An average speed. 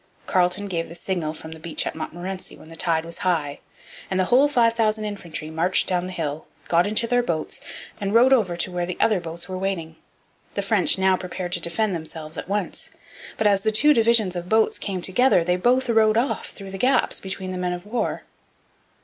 No: fast, 215 wpm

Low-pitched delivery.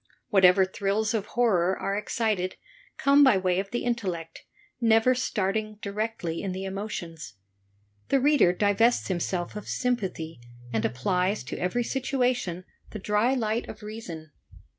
No: high, 205 Hz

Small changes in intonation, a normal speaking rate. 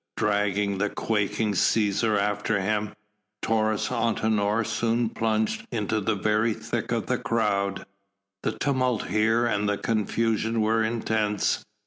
No: narrow, 1.6 semitones; slow, 125 wpm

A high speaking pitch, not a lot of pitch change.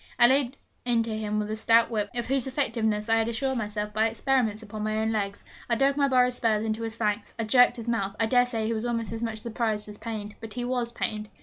Yes: high, 225 Hz; narrow, 2.0 semitones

